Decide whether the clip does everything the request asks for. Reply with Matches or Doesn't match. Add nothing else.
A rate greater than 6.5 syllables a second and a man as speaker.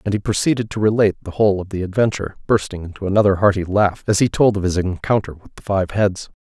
Matches